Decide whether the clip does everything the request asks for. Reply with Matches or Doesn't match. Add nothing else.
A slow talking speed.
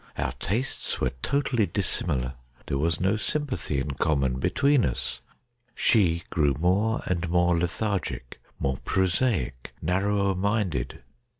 Matches